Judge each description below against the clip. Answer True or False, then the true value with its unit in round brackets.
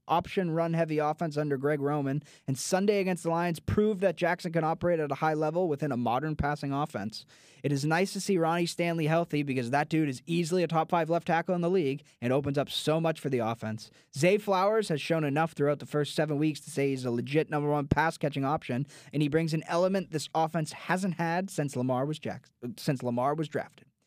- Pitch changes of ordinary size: True (3.0 semitones)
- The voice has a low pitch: False (155 Hz)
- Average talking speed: False (230 wpm)